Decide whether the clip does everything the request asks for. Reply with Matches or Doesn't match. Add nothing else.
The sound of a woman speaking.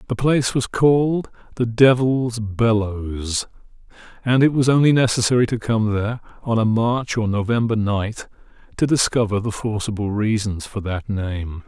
Doesn't match